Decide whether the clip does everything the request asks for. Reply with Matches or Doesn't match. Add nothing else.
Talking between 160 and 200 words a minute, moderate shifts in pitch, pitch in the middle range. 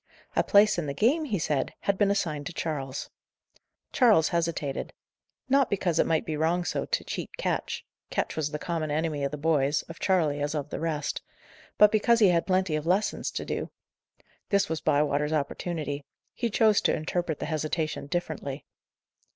Matches